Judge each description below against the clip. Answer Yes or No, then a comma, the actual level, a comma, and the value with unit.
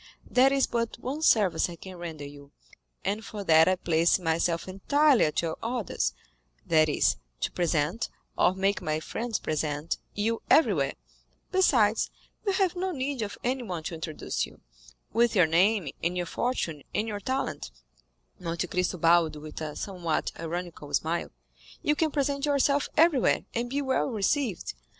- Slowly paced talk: No, average, 155 wpm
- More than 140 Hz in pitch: Yes, high, 190 Hz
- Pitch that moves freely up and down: Yes, wide, 7.5 semitones